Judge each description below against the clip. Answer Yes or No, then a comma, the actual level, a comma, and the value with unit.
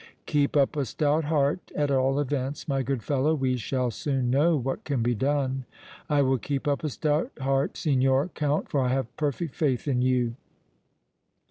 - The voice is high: No, low, 135 Hz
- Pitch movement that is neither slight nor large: No, narrow, 2.1 semitones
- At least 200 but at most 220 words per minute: No, average, 185 wpm